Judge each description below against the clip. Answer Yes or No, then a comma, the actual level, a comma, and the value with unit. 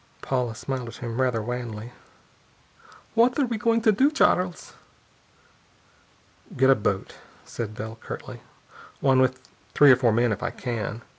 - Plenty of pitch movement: Yes, wide, 6.8 semitones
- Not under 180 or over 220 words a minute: No, average, 150 wpm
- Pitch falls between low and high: No, low, 125 Hz